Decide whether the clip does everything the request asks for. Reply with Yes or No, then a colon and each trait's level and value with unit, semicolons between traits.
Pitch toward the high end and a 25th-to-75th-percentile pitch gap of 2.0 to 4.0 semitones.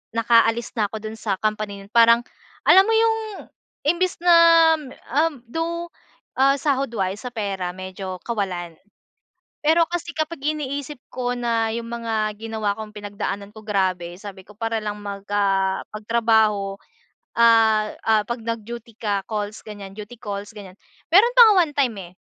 Yes: high, 220 Hz; average, 3.4 semitones